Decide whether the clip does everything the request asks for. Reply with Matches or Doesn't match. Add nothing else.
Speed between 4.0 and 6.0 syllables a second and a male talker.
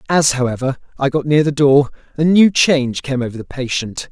Matches